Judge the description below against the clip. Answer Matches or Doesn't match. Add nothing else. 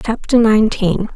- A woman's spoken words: Matches